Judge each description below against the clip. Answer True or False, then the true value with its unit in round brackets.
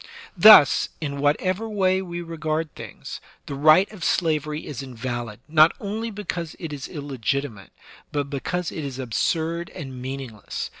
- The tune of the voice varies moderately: True (4.1 semitones)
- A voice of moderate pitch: True (155 Hz)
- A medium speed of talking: True (145 wpm)